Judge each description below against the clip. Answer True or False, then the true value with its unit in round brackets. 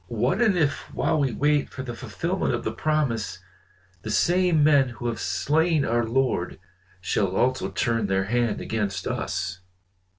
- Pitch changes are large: True (6.3 semitones)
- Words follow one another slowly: False (160 wpm)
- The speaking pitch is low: True (120 Hz)